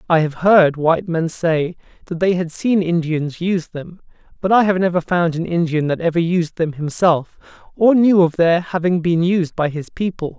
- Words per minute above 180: Yes, average, 200 wpm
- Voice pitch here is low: No, medium, 170 Hz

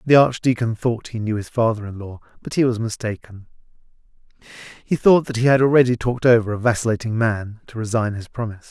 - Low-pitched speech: Yes, low, 115 Hz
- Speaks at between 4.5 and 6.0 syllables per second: No, 6.2 syllables/s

